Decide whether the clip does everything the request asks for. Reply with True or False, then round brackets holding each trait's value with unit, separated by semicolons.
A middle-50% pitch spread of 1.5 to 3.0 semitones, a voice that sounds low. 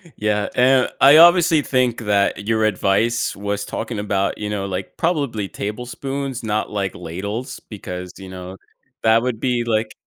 False (3.9 semitones; 110 Hz)